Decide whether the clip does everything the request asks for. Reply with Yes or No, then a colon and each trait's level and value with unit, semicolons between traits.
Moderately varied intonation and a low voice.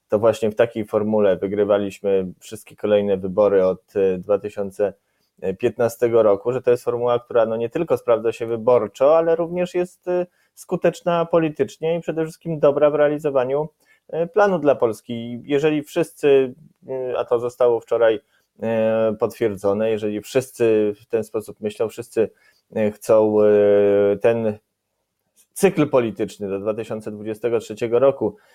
No: wide, 5.9 semitones; low, 115 Hz